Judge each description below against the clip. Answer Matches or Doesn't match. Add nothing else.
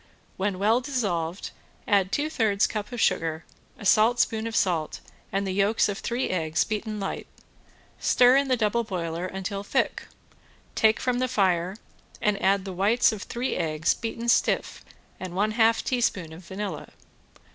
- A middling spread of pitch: Matches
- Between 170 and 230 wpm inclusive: Doesn't match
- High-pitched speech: Matches